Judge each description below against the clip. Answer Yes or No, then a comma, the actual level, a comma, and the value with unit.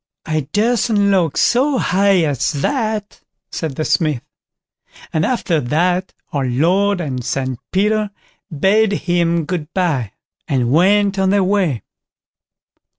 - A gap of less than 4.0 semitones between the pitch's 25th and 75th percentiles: No, average, 5.2 semitones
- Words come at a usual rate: No, slow, 125 wpm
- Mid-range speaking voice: Yes, medium, 180 Hz